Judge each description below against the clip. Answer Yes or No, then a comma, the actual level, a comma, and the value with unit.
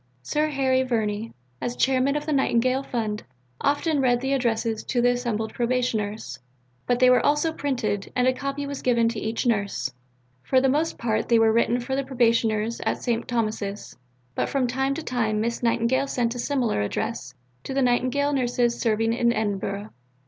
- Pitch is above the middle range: Yes, high, 240 Hz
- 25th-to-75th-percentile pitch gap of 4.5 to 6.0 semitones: No, average, 2.9 semitones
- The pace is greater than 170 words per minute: Yes, average, 180 wpm